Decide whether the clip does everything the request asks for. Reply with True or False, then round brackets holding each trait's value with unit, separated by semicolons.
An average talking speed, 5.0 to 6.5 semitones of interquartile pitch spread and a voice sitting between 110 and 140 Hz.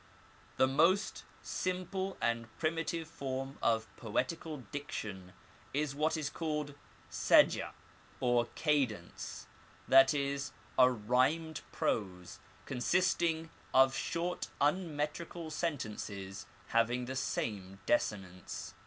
False (95 wpm; 5.6 semitones; 135 Hz)